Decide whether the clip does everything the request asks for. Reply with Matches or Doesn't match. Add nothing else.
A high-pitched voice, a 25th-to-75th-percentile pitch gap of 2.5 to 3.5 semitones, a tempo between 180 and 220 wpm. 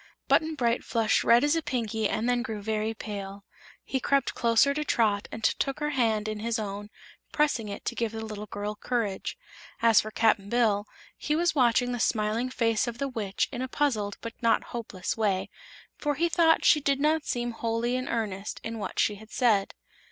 Matches